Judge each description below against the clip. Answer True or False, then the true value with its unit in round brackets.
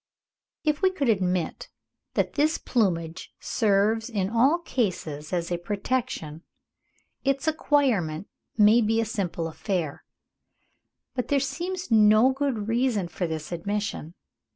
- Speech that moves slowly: True (125 wpm)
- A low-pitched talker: False (215 Hz)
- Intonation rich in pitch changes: True (6.9 semitones)